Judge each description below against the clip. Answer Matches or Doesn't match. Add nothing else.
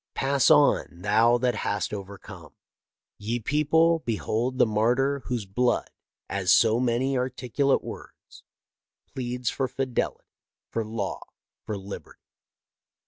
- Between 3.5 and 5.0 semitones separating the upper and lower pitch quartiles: Matches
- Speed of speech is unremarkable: Doesn't match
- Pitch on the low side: Matches